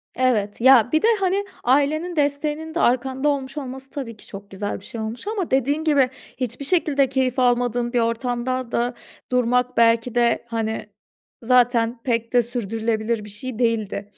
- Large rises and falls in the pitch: No, average, 2.8 semitones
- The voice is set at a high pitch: Yes, high, 245 Hz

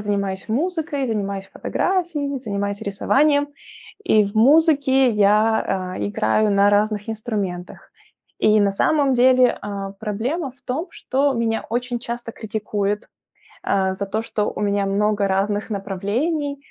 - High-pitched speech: Yes, high, 215 Hz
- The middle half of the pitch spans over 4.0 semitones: Yes, average, 4.7 semitones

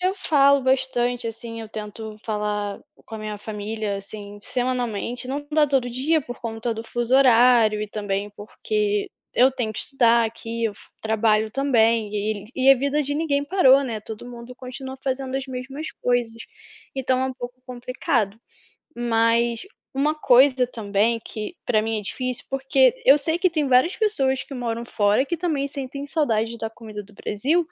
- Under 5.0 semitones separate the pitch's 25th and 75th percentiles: Yes, average, 3.6 semitones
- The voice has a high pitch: Yes, high, 245 Hz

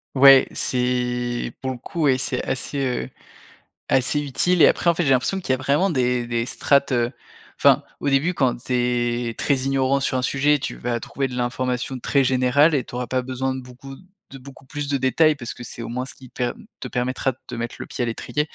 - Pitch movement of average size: No, narrow, 2.1 semitones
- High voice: No, low, 130 Hz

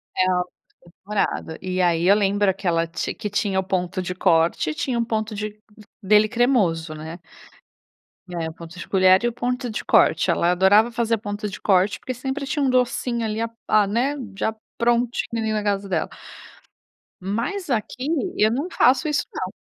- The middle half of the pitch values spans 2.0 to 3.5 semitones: No, average, 4.4 semitones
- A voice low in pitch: No, high, 210 Hz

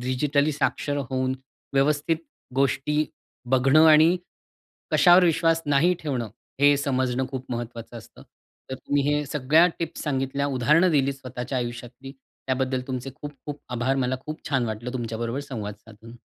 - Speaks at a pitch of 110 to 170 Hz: Yes, low, 135 Hz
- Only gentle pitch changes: No, average, 3.0 semitones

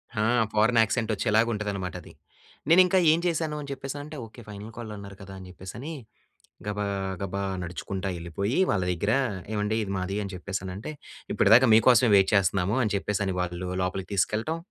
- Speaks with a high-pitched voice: No, low, 105 Hz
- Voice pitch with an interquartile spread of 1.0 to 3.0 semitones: No, average, 3.5 semitones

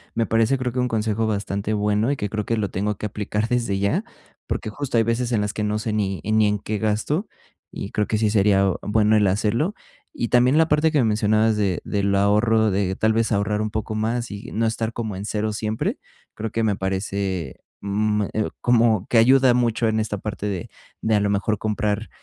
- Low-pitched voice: Yes, low, 110 Hz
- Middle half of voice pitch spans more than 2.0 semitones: No, narrow, 1.7 semitones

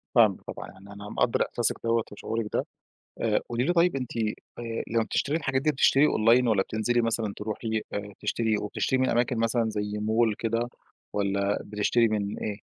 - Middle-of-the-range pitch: No, low, 115 Hz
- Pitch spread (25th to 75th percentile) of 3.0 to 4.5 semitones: No, narrow, 2.4 semitones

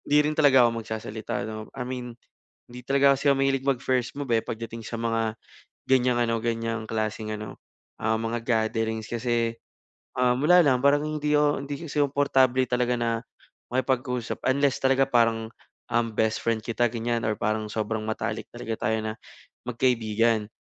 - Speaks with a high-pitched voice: No, low, 120 Hz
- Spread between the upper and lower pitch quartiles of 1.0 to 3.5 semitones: Yes, average, 2.8 semitones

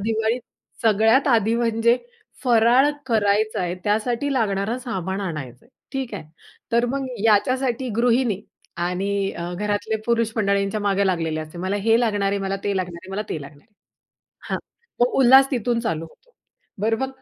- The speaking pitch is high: Yes, high, 220 Hz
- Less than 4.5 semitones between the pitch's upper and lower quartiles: Yes, average, 3.4 semitones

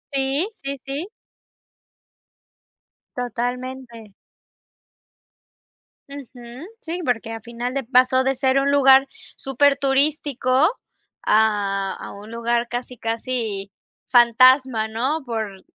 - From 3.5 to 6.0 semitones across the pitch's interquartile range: No, average, 2.9 semitones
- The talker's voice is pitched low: No, very high, 255 Hz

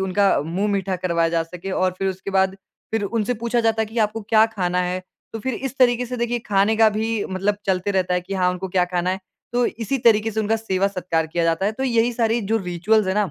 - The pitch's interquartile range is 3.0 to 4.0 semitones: Yes, average, 3.5 semitones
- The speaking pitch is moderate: No, high, 200 Hz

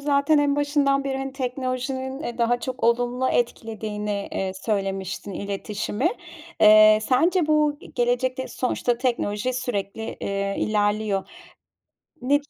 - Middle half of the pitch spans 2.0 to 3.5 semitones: No, average, 4.2 semitones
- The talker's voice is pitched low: No, high, 245 Hz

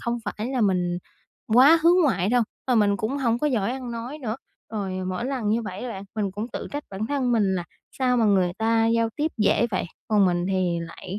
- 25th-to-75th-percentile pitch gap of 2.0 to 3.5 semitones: No, average, 4.3 semitones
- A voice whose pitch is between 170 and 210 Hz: No, high, 225 Hz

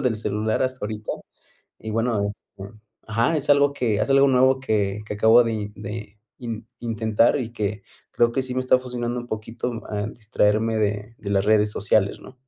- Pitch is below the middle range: Yes, low, 110 Hz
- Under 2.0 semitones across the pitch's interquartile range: No, average, 2.7 semitones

